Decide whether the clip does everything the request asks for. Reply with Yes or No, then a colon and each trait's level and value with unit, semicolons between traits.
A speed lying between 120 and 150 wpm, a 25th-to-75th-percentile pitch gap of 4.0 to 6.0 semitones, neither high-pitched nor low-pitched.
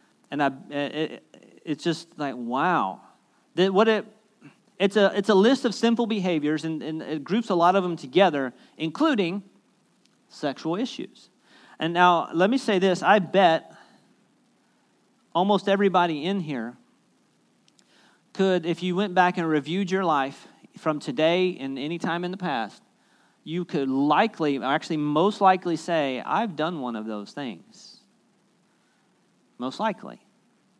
Yes: average, 145 wpm; average, 4.5 semitones; medium, 180 Hz